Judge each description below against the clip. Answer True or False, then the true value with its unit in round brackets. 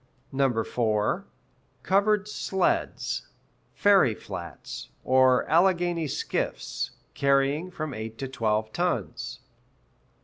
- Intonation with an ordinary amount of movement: False (7.8 semitones)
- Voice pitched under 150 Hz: True (135 Hz)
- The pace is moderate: False (80 wpm)